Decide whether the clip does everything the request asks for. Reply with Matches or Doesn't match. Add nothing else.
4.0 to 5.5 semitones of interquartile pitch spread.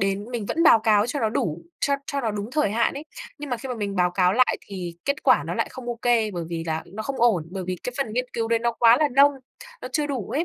Matches